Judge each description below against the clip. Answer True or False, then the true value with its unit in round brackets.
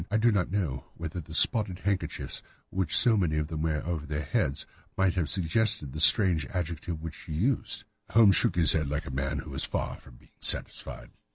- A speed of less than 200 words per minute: False (205 wpm)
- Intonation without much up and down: False (4.1 semitones)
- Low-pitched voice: True (85 Hz)